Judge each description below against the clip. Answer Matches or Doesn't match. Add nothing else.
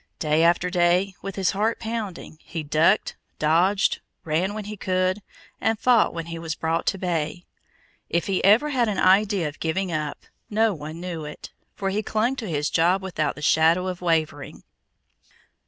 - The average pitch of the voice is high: Doesn't match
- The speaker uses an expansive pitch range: Doesn't match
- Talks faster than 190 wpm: Doesn't match